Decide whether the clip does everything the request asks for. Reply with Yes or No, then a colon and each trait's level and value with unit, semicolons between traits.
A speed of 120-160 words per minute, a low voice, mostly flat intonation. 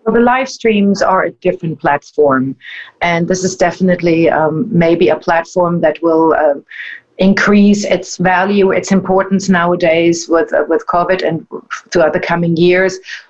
No: average, 155 wpm; medium, 180 Hz; narrow, 2.3 semitones